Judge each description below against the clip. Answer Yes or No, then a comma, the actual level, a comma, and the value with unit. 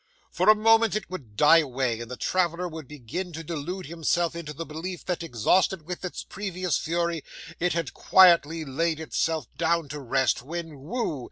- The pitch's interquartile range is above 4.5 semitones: No, average, 3.2 semitones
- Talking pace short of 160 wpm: No, average, 180 wpm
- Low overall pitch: No, medium, 165 Hz